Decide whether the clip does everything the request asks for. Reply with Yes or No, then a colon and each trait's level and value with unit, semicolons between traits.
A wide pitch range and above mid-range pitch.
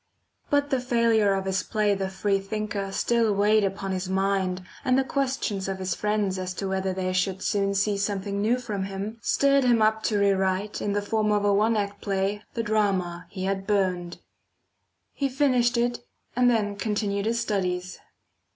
No: narrow, 2.4 semitones; high, 200 Hz